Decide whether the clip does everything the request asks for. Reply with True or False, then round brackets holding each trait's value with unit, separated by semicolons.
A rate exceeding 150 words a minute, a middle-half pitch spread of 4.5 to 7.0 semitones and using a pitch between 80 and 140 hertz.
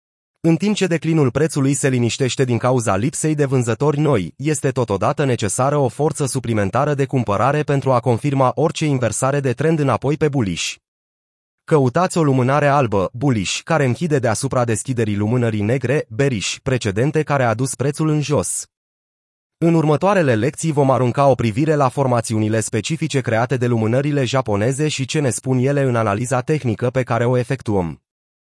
False (160 wpm; 3.8 semitones; 135 Hz)